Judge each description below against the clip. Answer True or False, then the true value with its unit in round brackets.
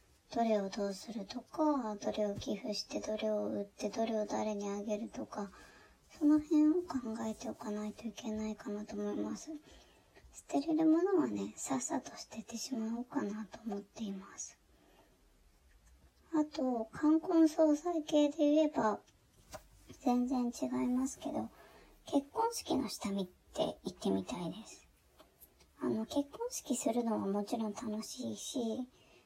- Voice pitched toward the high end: True (230 Hz)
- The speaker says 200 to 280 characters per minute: True (275 characters per minute)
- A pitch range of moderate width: False (5.8 semitones)